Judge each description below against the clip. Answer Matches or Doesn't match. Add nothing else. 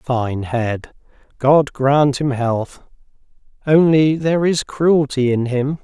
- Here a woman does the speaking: Doesn't match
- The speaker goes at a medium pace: Doesn't match